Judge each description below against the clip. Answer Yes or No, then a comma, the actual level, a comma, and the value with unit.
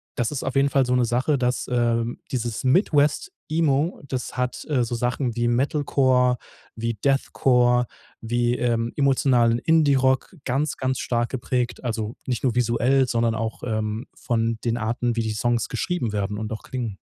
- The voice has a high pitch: No, low, 125 Hz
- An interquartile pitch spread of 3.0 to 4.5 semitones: No, narrow, 2.4 semitones